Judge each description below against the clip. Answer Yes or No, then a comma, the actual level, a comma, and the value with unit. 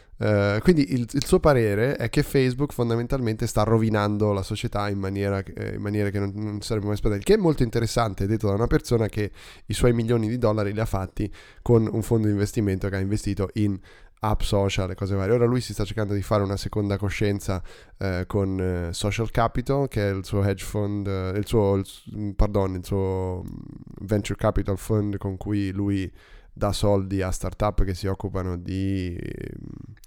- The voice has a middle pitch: No, low, 105 Hz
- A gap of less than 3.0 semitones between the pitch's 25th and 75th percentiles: Yes, narrow, 2.6 semitones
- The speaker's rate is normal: No, fast, 200 wpm